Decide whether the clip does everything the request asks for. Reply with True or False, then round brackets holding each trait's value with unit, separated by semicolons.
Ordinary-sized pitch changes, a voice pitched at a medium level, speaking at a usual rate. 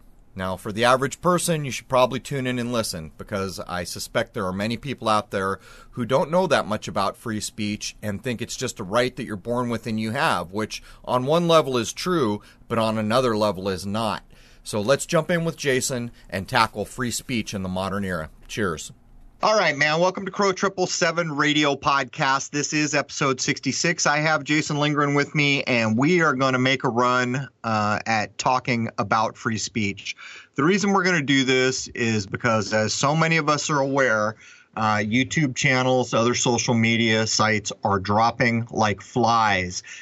False (4.8 semitones; 125 Hz; 195 wpm)